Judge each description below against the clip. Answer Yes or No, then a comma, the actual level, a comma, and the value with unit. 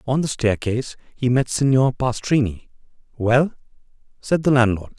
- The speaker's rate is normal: No, slow, 130 wpm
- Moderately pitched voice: No, low, 125 Hz